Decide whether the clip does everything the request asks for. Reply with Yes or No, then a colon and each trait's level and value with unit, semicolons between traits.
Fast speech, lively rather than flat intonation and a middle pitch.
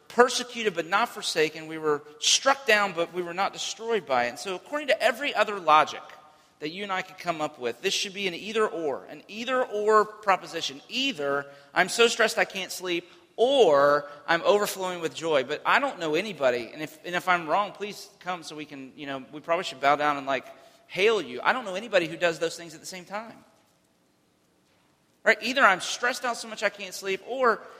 Yes: fast, 235 wpm; wide, 5.7 semitones; medium, 180 Hz